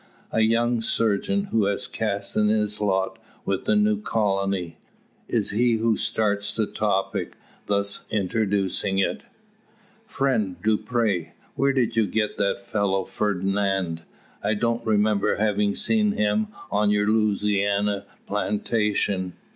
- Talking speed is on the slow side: Yes, slow, 125 wpm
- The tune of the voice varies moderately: No, narrow, 2.0 semitones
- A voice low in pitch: Yes, low, 105 Hz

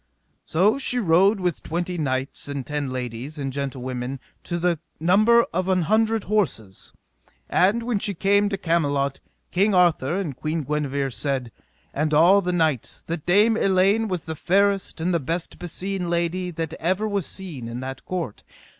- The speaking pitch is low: No, medium, 170 Hz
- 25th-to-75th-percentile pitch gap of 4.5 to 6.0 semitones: Yes, wide, 5.4 semitones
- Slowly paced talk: No, average, 165 wpm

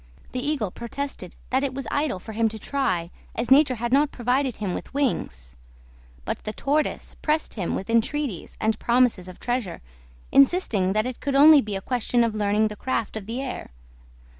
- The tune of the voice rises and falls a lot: No, average, 4.5 semitones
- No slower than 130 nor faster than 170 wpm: No, average, 190 wpm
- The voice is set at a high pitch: Yes, high, 240 Hz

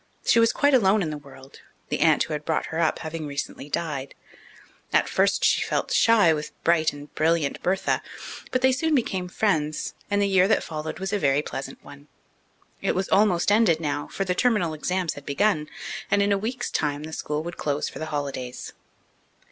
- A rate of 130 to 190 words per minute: No, fast, 205 wpm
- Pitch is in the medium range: Yes, medium, 165 Hz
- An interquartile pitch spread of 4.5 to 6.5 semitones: Yes, average, 5.2 semitones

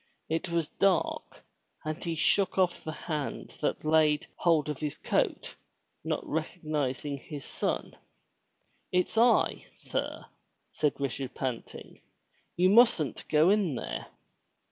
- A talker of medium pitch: Yes, medium, 155 Hz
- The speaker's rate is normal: No, slow, 130 wpm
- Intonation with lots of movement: No, average, 3.5 semitones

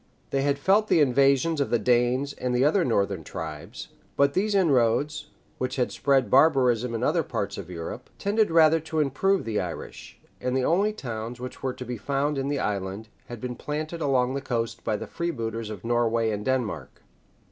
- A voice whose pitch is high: No, low, 130 Hz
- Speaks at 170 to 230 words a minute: Yes, average, 190 wpm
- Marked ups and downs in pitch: No, average, 4.4 semitones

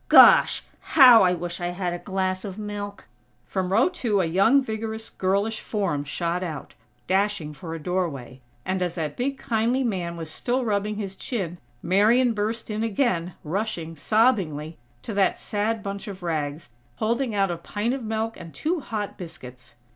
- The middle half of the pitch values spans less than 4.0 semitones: No, average, 4.4 semitones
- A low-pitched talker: No, high, 195 Hz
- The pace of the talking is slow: No, average, 170 wpm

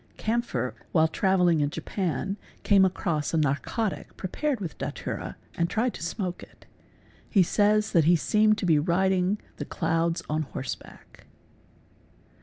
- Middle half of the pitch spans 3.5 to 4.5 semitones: Yes, average, 3.9 semitones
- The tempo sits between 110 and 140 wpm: Yes, slow, 135 wpm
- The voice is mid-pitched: Yes, medium, 180 Hz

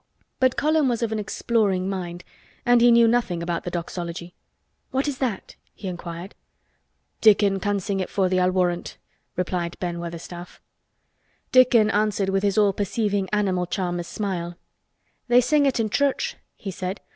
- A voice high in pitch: Yes, high, 195 Hz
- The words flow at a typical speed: Yes, average, 160 wpm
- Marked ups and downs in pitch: No, average, 4.5 semitones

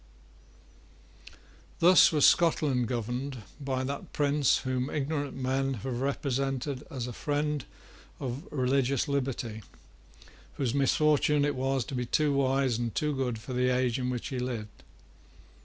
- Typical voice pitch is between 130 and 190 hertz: Yes, low, 135 Hz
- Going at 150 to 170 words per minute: No, average, 140 wpm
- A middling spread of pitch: No, narrow, 2.2 semitones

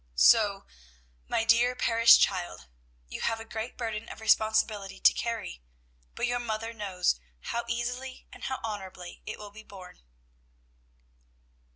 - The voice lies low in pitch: No, high, 220 Hz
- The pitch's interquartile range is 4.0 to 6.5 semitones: No, average, 2.7 semitones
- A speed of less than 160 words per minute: Yes, average, 140 wpm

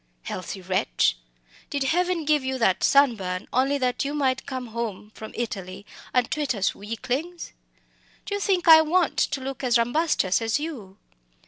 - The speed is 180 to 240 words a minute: No, average, 165 wpm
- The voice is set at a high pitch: Yes, very high, 255 Hz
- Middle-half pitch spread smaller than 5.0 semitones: No, wide, 5.6 semitones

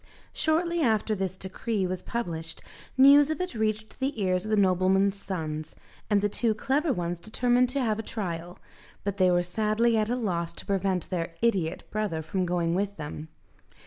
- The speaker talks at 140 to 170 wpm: No, average, 180 wpm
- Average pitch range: Yes, average, 4.5 semitones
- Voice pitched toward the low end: No, high, 200 Hz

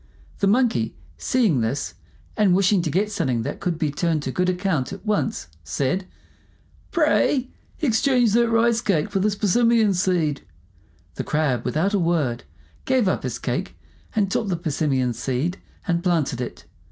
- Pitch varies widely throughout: Yes, wide, 6.2 semitones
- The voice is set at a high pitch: No, medium, 180 Hz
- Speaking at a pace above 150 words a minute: Yes, average, 160 wpm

